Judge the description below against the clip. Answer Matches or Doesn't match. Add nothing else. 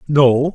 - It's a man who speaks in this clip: Matches